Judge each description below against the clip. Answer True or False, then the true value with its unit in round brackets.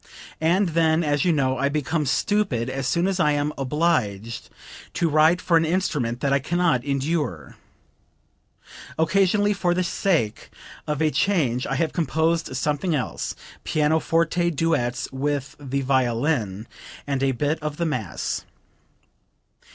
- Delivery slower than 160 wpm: True (145 wpm)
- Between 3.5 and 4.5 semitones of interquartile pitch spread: True (4.1 semitones)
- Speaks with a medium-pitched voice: True (150 Hz)